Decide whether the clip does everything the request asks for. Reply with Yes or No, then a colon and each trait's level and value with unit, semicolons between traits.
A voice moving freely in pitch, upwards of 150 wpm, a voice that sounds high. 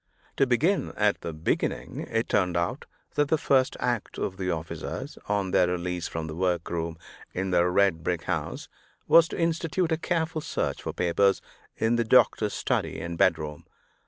No: wide, 7.0 semitones; average, 170 wpm; very low, 95 Hz